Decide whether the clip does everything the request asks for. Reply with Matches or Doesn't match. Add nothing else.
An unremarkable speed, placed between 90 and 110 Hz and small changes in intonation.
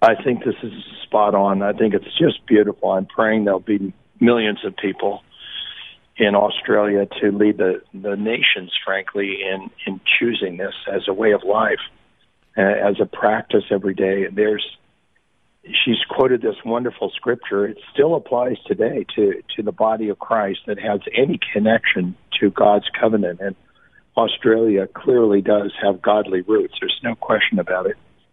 Matches